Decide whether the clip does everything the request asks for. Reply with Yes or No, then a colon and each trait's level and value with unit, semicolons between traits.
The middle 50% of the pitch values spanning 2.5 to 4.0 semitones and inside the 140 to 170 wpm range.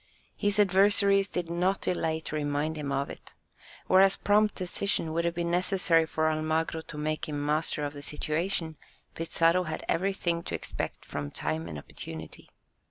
Yes: average, 3.5 semitones; average, 165 wpm